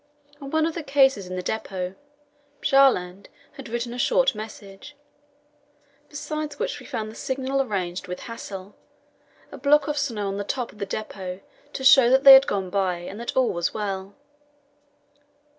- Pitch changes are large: Yes, wide, 5.9 semitones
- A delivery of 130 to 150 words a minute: No, average, 175 wpm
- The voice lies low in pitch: No, high, 230 Hz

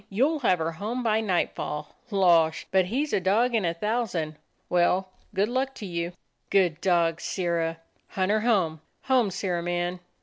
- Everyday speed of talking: Yes, average, 170 wpm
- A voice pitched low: No, medium, 185 Hz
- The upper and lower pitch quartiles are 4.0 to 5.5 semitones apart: Yes, average, 4.3 semitones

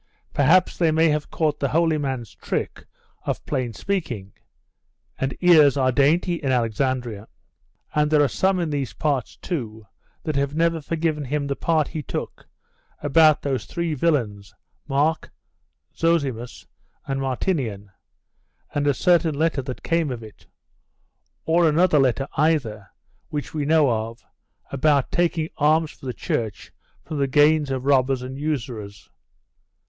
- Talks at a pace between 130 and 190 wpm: Yes, average, 145 wpm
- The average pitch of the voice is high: No, medium, 145 Hz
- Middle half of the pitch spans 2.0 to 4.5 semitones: Yes, average, 3.8 semitones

